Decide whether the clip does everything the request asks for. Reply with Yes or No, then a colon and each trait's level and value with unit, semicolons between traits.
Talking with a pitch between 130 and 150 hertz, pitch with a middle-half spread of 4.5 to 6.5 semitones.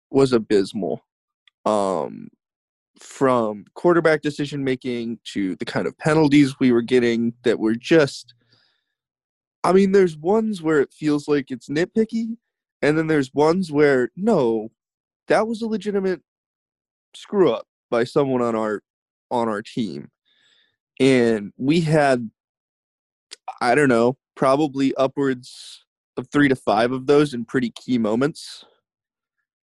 Yes: medium, 140 Hz; average, 5.1 semitones